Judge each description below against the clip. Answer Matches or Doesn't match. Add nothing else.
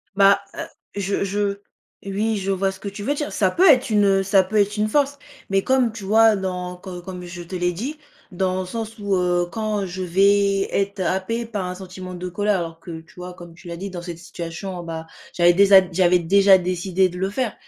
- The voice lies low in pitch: Doesn't match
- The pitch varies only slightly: Matches